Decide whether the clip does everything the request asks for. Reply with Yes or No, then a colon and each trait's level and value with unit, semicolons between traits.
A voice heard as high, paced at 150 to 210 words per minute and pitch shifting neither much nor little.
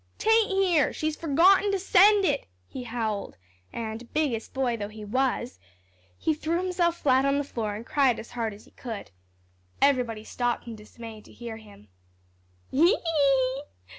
No: very high, 260 Hz; average, 165 wpm; wide, 6.2 semitones